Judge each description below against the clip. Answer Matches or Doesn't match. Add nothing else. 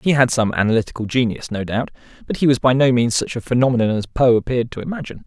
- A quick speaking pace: Matches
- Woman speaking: Doesn't match